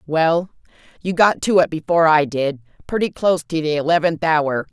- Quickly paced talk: No, average, 165 wpm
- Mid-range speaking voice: Yes, medium, 160 Hz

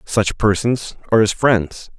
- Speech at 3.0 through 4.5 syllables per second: Yes, 4.2 syllables/s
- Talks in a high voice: No, low, 105 Hz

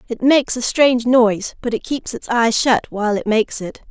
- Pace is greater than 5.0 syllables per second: Yes, 5.5 syllables/s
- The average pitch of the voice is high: Yes, high, 235 Hz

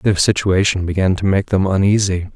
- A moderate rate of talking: Yes, average, 180 wpm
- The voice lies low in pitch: Yes, very low, 95 Hz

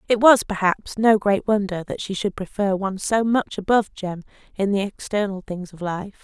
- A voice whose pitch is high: Yes, high, 200 Hz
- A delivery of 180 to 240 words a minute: Yes, average, 200 wpm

